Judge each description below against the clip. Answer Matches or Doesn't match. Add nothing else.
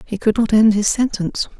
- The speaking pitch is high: Matches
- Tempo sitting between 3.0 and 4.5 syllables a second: Doesn't match